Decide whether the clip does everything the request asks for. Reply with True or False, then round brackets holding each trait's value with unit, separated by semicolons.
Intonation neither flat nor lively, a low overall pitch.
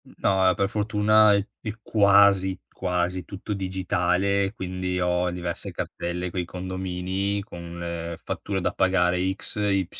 False (1.9 semitones; 95 Hz)